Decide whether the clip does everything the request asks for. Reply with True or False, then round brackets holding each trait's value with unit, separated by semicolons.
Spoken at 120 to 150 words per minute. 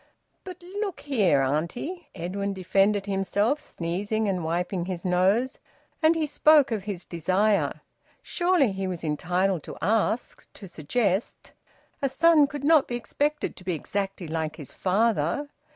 True (145 wpm)